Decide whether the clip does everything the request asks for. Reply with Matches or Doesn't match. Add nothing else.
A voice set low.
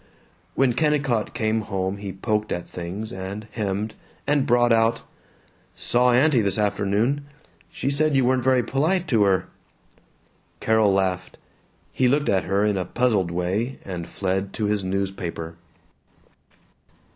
Matches